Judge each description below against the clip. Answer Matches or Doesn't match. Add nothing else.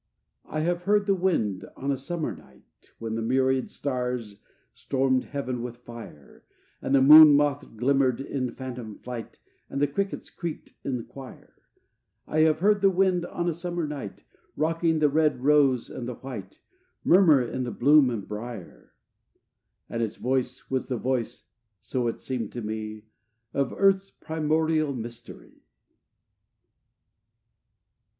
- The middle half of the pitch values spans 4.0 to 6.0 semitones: Matches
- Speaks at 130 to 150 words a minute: Matches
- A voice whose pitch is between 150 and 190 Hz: Doesn't match